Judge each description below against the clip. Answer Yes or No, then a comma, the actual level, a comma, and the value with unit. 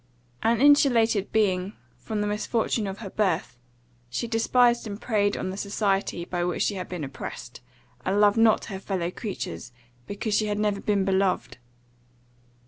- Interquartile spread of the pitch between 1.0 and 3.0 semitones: Yes, narrow, 2.6 semitones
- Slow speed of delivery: No, average, 160 wpm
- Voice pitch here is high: Yes, high, 205 Hz